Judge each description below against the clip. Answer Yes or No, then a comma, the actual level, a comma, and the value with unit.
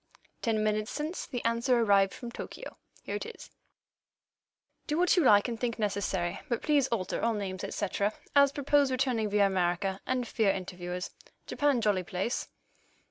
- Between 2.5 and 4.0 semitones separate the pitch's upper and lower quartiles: No, average, 4.7 semitones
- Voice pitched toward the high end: Yes, high, 220 Hz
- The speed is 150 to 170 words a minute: Yes, average, 165 wpm